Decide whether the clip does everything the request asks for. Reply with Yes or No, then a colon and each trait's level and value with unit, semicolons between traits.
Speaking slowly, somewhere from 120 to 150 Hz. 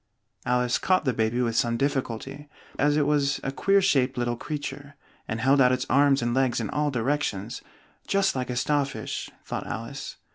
No: average, 185 wpm; low, 135 Hz